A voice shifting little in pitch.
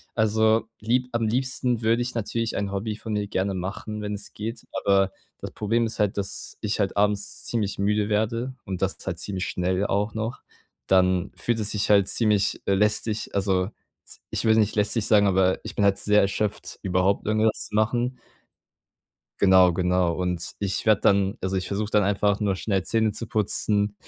Yes: narrow, 2.2 semitones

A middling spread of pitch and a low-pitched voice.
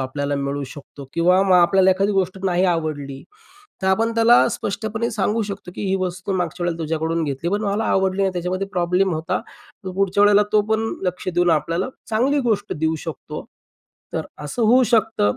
No: average, 3.6 semitones; medium, 185 Hz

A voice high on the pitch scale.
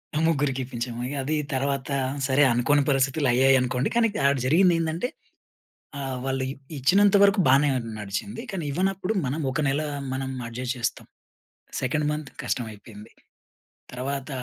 No: low, 135 Hz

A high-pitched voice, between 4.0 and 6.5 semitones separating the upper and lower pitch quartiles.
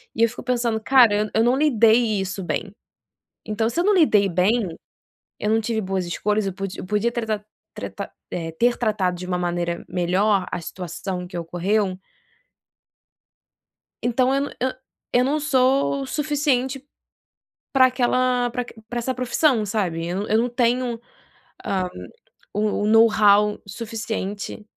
Yes: high, 220 Hz; average, 4.4 semitones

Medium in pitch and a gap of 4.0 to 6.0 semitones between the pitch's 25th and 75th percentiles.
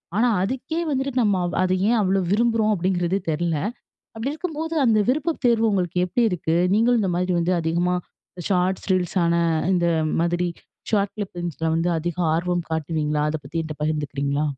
Yes: medium, 180 Hz; average, 4.7 semitones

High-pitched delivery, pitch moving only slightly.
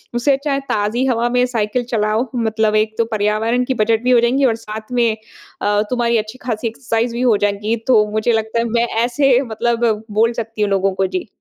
Yes: high, 230 Hz; narrow, 2.2 semitones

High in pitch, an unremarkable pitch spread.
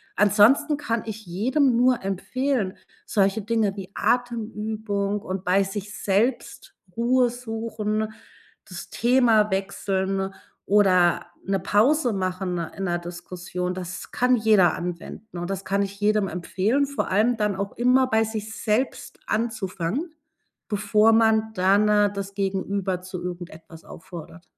Yes: high, 205 Hz; average, 3.0 semitones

